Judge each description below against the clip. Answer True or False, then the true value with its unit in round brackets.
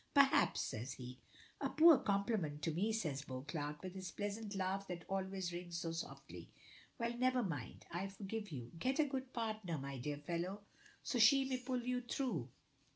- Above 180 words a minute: False (175 wpm)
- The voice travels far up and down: True (6.5 semitones)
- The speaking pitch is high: True (195 Hz)